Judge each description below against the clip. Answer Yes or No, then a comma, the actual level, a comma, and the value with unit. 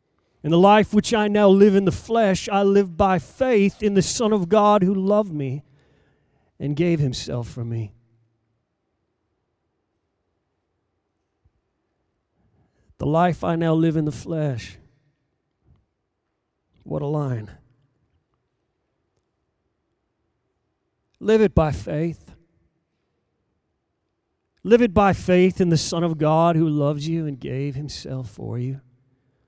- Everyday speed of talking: No, slow, 120 wpm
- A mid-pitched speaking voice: Yes, medium, 155 Hz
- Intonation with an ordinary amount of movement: No, wide, 7.3 semitones